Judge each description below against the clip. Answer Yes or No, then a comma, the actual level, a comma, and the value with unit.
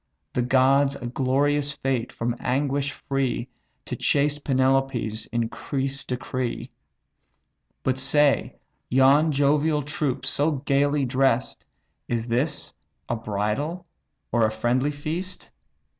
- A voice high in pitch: No, low, 135 Hz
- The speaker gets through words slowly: Yes, slow, 110 wpm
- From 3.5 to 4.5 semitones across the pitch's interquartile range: No, average, 2.7 semitones